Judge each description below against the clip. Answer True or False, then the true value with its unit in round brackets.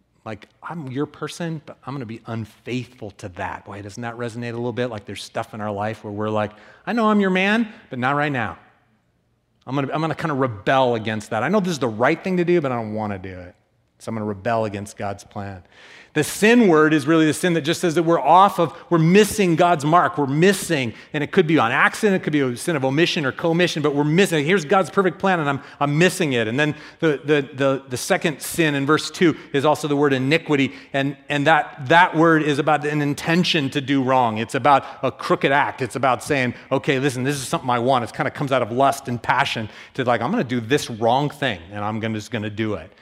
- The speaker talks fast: True (255 wpm)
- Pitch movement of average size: False (5.8 semitones)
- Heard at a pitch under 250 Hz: True (140 Hz)